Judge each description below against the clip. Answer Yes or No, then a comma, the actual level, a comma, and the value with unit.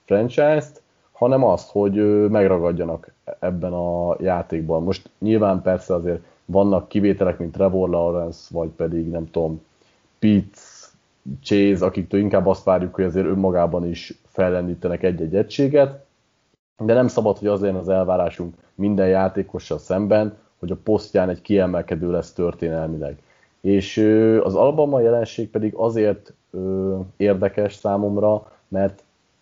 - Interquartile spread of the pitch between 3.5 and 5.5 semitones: No, average, 3.1 semitones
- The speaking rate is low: No, average, 125 wpm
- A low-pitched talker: Yes, very low, 95 Hz